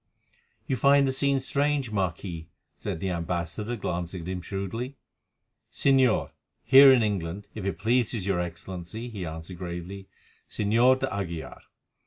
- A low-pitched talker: Yes, low, 100 Hz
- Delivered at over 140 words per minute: No, slow, 135 wpm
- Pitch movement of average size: No, wide, 6.3 semitones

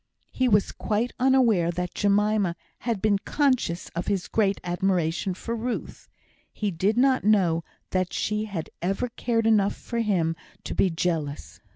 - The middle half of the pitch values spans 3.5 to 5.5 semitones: Yes, average, 4.2 semitones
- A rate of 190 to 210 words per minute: No, average, 155 wpm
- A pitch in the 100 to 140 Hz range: No, high, 200 Hz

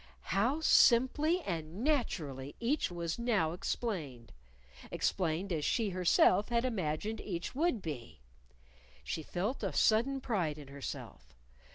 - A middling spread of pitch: No, wide, 7.2 semitones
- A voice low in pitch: No, high, 190 Hz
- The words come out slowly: Yes, slow, 125 wpm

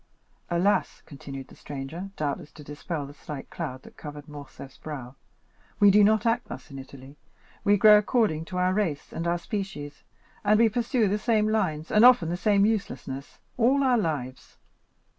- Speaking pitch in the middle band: Yes, medium, 175 Hz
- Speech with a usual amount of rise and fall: No, wide, 6.5 semitones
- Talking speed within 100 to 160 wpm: No, average, 175 wpm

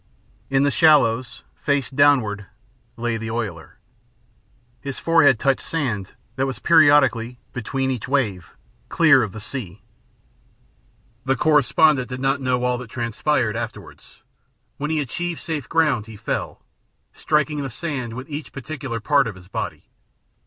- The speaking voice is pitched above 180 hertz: No, low, 130 Hz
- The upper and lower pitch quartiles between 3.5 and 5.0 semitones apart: Yes, average, 4.0 semitones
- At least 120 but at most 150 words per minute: Yes, average, 140 wpm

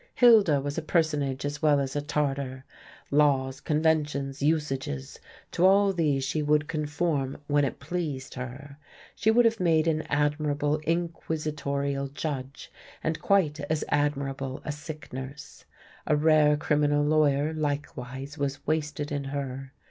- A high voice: No, medium, 145 Hz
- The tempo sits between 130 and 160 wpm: Yes, average, 140 wpm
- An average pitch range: No, narrow, 2.0 semitones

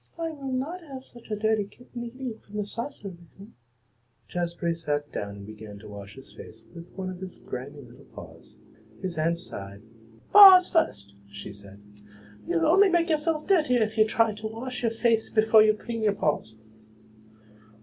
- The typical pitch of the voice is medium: No, high, 210 Hz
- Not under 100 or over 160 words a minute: No, average, 180 wpm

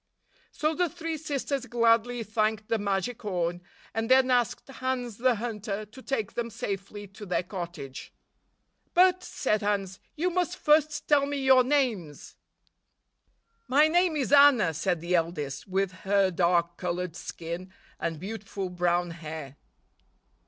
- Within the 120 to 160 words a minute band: Yes, average, 140 wpm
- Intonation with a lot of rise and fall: Yes, wide, 6.6 semitones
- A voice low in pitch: No, high, 215 Hz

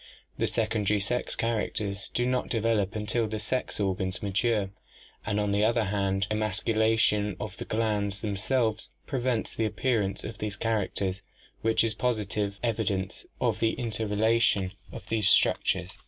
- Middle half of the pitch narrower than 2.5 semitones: Yes, narrow, 2.1 semitones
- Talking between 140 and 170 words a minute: Yes, average, 150 wpm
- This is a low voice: Yes, low, 105 Hz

